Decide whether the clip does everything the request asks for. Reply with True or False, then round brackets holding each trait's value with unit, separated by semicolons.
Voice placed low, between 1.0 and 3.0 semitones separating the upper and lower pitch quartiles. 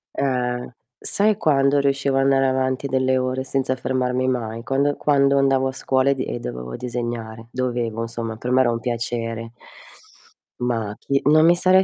True (130 Hz; 2.5 semitones)